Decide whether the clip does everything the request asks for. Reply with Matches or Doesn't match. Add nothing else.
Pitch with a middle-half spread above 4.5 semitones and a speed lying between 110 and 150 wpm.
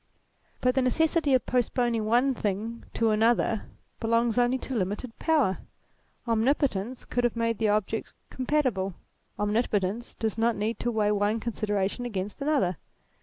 Doesn't match